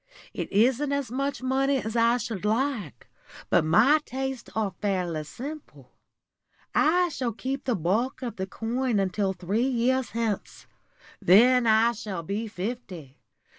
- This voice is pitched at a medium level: No, high, 230 Hz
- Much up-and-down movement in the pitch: No, average, 4.7 semitones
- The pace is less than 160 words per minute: Yes, average, 140 wpm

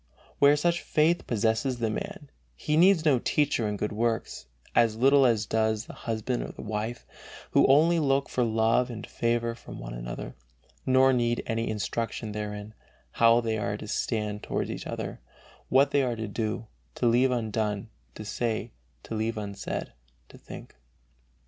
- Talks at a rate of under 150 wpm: No, average, 170 wpm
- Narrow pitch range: No, average, 3.2 semitones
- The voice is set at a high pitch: No, low, 115 Hz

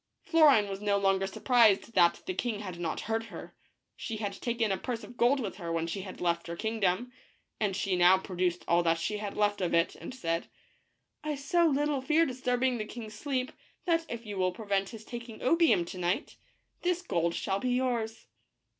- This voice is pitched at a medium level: No, high, 215 Hz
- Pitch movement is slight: No, average, 5.1 semitones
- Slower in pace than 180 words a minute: No, average, 200 wpm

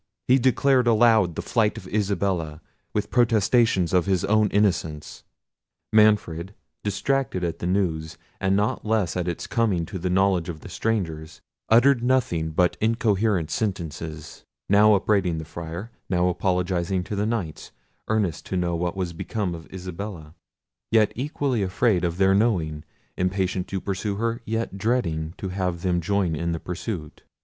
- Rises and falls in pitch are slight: No, average, 4.0 semitones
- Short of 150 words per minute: No, average, 155 wpm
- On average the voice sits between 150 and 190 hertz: No, very low, 95 Hz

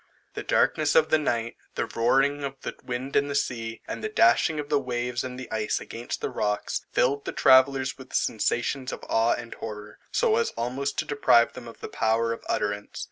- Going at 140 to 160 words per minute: No, average, 200 wpm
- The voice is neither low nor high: No, low, 125 Hz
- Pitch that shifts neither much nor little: Yes, average, 3.4 semitones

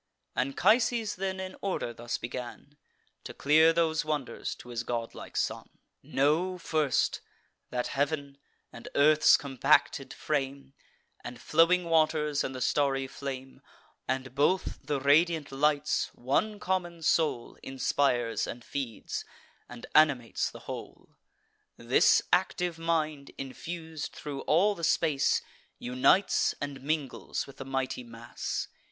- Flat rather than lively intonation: No, average, 3.7 semitones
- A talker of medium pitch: Yes, medium, 145 Hz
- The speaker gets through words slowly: Yes, slow, 120 wpm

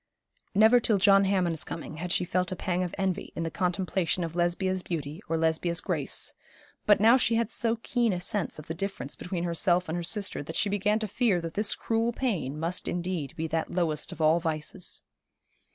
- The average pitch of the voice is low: No, medium, 180 Hz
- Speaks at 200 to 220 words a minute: Yes, fast, 205 wpm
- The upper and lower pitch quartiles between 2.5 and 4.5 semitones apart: Yes, average, 3.6 semitones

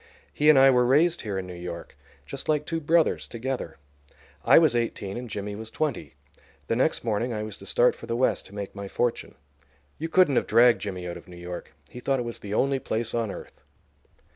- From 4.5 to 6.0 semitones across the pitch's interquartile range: Yes, average, 5.0 semitones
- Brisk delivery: Yes, fast, 220 wpm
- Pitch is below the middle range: Yes, low, 115 Hz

